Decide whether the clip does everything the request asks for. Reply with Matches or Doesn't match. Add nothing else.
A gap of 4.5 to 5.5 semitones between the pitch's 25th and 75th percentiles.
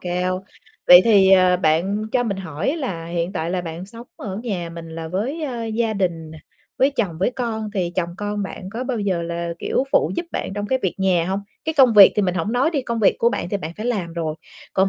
Matches